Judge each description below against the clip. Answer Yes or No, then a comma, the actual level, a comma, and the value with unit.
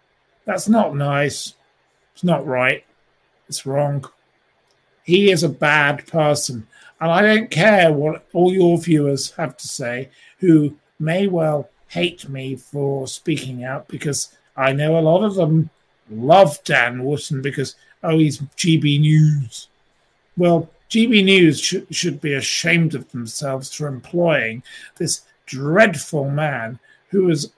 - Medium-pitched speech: Yes, medium, 150 Hz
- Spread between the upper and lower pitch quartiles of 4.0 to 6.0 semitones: No, average, 3.5 semitones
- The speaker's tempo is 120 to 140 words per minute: Yes, slow, 135 wpm